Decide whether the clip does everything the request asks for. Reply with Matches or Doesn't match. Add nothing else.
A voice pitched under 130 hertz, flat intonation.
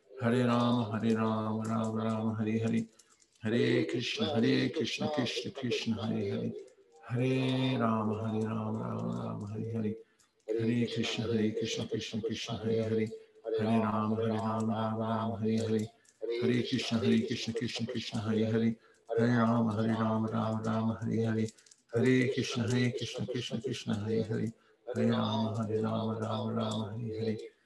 Matches